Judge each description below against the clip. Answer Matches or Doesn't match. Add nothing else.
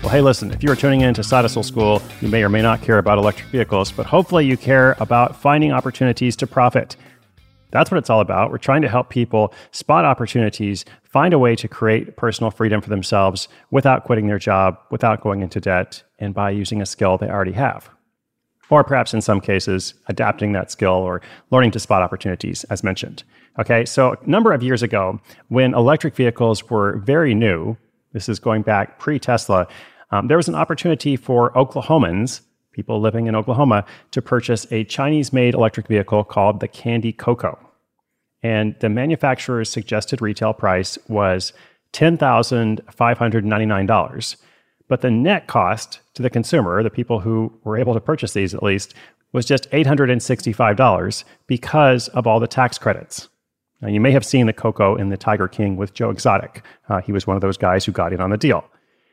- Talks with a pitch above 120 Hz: Doesn't match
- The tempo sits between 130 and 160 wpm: Doesn't match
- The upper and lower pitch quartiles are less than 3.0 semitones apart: Doesn't match